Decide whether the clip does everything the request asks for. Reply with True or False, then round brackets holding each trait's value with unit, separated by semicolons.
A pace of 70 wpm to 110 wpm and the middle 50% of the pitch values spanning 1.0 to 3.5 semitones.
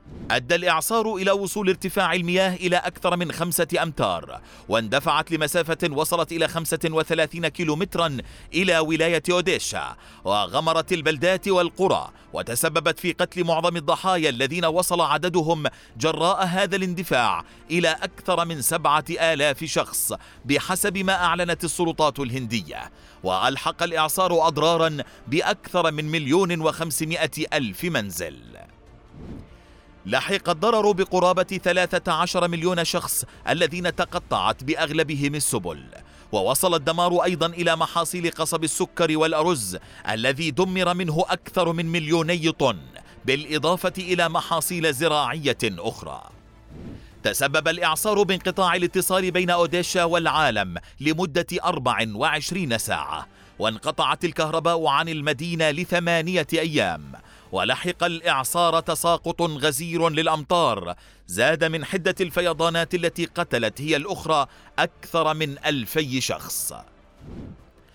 True (105 wpm; 2.5 semitones)